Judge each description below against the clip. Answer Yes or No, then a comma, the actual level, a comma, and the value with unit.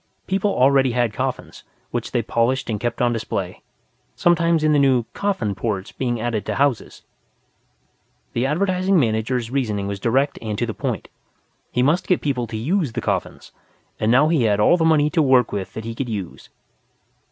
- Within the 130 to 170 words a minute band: No, average, 185 wpm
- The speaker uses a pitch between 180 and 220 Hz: No, low, 125 Hz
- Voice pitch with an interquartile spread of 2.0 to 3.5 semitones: No, average, 5.2 semitones